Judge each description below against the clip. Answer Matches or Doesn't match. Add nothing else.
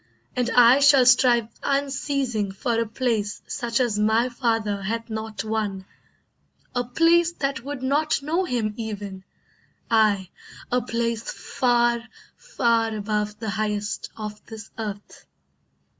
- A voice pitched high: Matches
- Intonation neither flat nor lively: Matches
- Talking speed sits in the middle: Doesn't match